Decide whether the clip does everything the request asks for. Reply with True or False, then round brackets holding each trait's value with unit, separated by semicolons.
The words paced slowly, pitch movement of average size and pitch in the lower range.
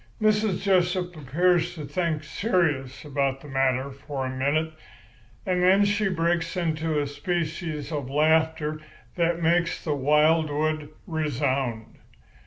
False (125 wpm; 3.4 semitones; 155 Hz)